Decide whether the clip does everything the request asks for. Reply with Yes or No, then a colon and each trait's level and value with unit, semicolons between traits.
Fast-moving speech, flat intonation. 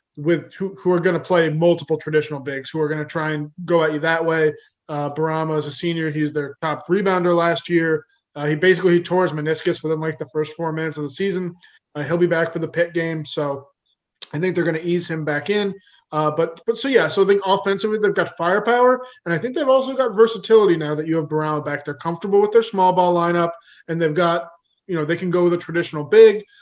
No: fast, 250 wpm; average, 3.0 semitones